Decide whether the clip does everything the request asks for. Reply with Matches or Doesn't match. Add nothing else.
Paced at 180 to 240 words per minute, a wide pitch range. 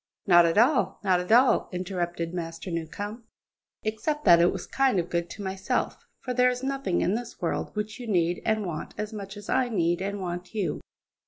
Doesn't match